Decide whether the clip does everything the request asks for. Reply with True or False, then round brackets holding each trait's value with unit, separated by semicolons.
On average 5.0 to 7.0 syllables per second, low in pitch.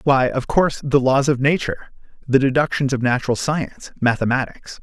True (5.5 syllables/s; 130 Hz)